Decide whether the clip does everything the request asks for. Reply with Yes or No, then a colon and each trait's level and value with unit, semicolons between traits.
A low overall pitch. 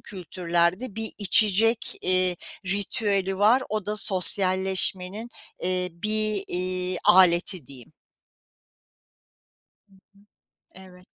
No: high, 190 Hz